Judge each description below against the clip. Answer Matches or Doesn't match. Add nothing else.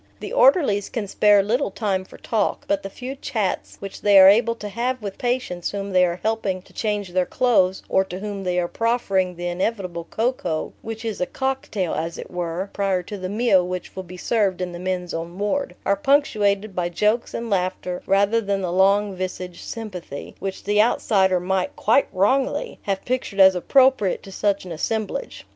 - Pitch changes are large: Doesn't match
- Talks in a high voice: Matches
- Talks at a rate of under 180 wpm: Doesn't match